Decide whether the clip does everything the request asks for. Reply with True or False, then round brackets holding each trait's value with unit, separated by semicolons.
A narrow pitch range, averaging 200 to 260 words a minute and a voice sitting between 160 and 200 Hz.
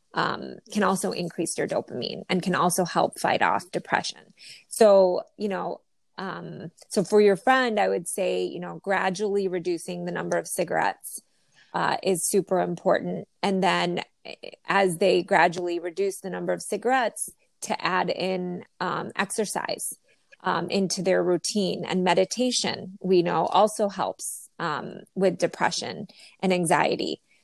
False (2.2 semitones; 145 wpm; 190 Hz)